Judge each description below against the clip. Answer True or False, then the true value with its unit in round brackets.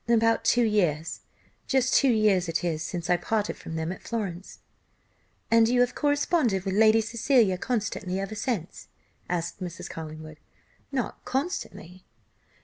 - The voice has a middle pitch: False (205 Hz)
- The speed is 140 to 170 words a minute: True (145 wpm)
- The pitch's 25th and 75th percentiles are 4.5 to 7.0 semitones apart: True (5.1 semitones)